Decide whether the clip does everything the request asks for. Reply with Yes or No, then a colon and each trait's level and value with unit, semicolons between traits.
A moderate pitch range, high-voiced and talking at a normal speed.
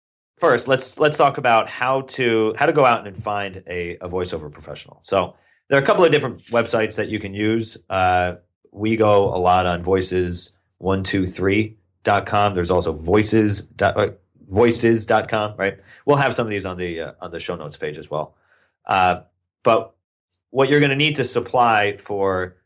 No: average, 4.1 semitones; low, 100 Hz; average, 175 wpm